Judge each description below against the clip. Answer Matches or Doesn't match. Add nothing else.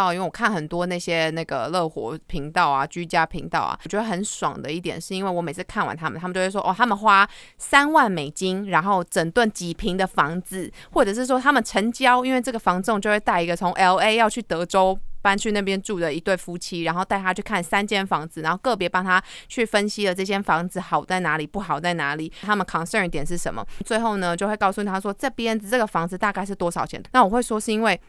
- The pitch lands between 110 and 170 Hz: Doesn't match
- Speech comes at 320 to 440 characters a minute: Matches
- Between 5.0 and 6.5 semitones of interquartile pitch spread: Doesn't match